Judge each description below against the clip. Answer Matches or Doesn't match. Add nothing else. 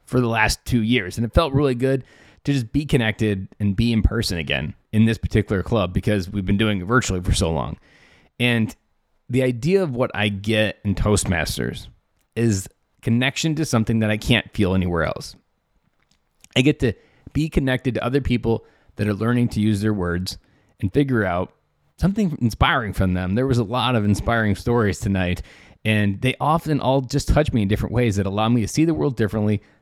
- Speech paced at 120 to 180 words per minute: Doesn't match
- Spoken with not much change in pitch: Doesn't match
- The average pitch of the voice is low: Matches